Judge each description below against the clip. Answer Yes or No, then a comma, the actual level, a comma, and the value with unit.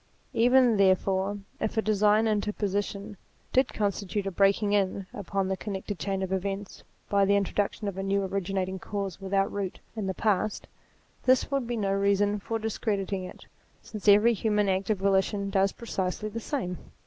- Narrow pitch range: Yes, narrow, 1.6 semitones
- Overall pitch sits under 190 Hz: No, high, 200 Hz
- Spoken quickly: No, average, 170 wpm